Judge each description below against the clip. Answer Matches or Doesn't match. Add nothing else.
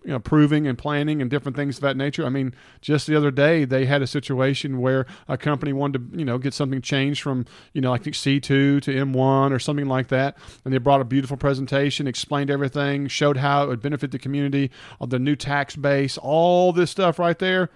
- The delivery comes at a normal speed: Doesn't match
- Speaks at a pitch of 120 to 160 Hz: Matches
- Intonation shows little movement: Matches